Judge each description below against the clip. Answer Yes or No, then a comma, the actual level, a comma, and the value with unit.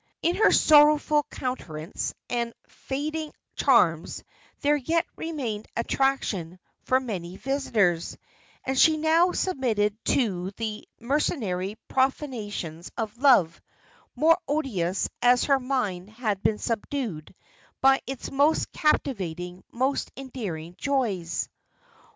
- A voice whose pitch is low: No, high, 245 Hz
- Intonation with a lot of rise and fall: Yes, wide, 6.6 semitones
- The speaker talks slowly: Yes, slow, 105 wpm